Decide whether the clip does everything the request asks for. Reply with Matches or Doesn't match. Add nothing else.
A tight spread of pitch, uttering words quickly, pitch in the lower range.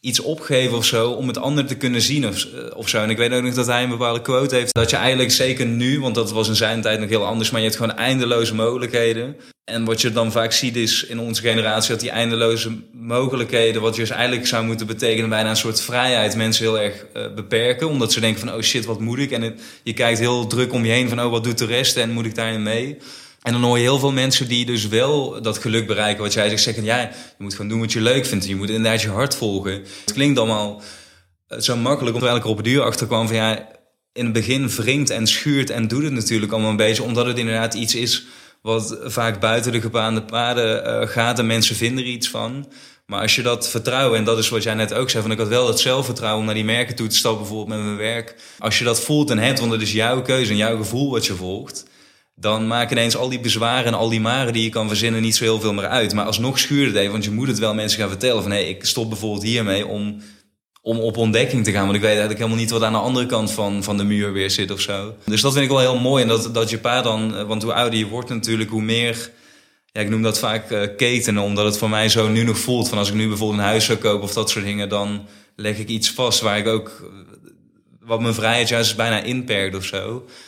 Matches